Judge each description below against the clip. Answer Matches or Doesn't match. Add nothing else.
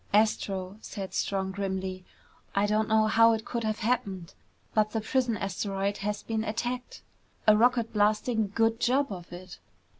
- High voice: Matches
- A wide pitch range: Doesn't match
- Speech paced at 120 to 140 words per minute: Doesn't match